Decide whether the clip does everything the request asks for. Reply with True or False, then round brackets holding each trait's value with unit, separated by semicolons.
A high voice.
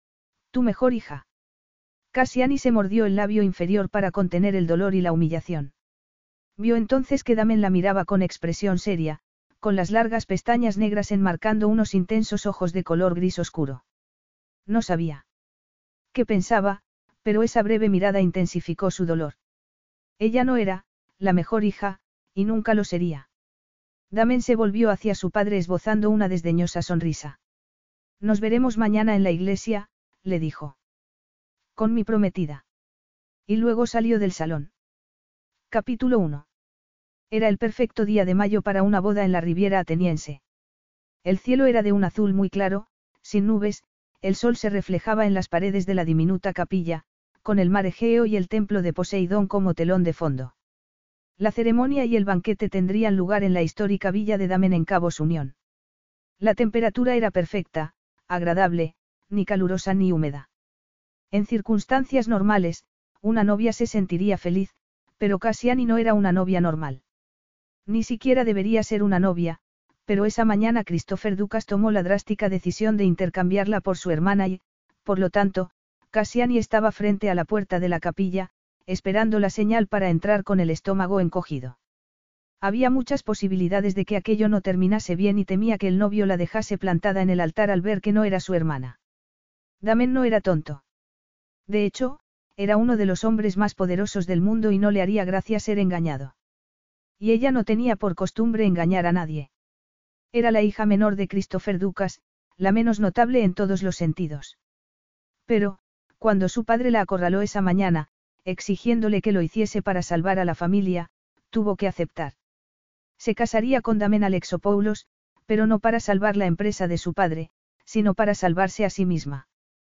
True (200 Hz)